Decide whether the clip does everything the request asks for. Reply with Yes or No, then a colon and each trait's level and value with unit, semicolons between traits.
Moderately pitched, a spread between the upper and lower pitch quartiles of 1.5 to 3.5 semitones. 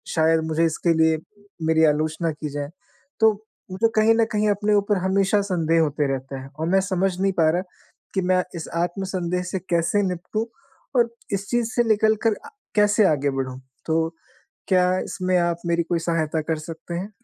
No: medium, 175 Hz; average, 3.9 semitones